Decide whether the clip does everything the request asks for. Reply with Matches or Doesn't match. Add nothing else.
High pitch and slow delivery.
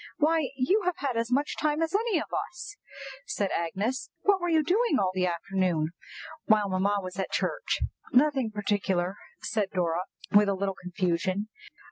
Doesn't match